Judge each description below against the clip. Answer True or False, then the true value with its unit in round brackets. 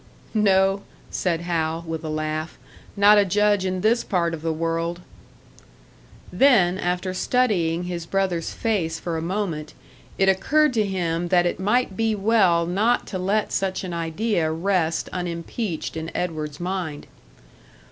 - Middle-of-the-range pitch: True (180 Hz)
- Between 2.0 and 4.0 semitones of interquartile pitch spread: True (3.3 semitones)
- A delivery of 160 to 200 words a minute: False (145 wpm)